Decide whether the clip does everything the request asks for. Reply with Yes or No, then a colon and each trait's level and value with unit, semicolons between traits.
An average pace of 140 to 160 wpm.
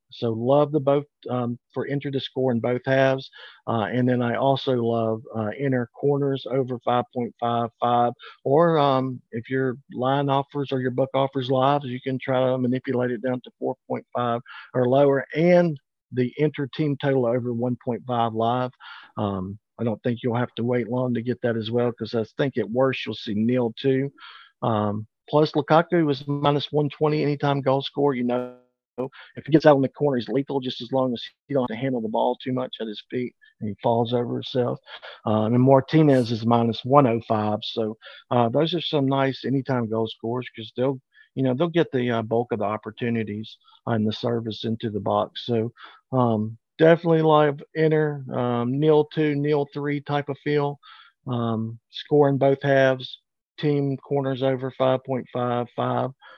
No: average, 185 wpm